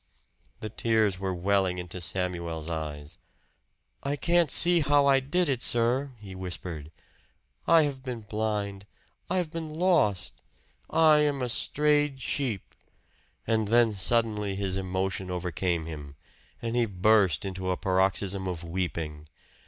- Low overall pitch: Yes, low, 100 Hz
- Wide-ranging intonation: Yes, wide, 6.5 semitones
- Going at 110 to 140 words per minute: Yes, slow, 135 wpm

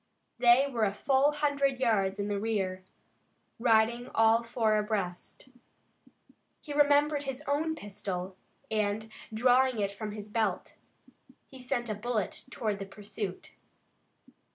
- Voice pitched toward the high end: Yes, high, 225 Hz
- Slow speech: Yes, slow, 130 wpm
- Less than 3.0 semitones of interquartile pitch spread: No, average, 4.2 semitones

